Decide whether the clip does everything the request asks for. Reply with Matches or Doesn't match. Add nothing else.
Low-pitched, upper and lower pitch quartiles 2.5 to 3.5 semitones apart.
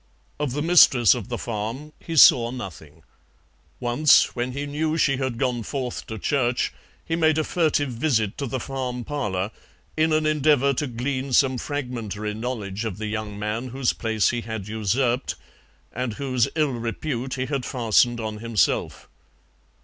Doesn't match